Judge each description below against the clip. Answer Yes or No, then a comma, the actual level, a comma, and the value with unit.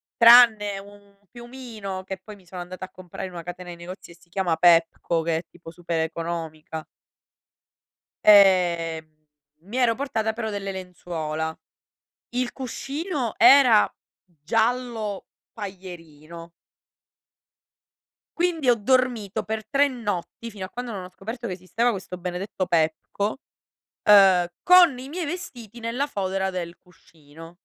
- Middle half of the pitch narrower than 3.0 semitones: No, average, 5.2 semitones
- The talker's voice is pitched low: No, high, 195 Hz